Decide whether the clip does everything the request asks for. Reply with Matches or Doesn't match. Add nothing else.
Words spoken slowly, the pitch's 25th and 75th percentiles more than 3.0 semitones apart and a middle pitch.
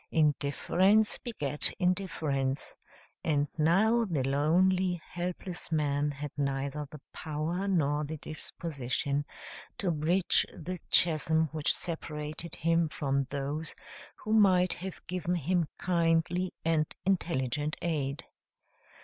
Matches